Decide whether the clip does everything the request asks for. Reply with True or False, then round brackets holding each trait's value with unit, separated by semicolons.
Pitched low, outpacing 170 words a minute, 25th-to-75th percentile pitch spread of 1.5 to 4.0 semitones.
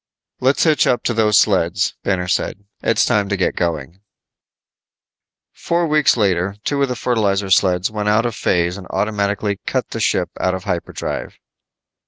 False (100 Hz; 165 wpm; 3.3 semitones)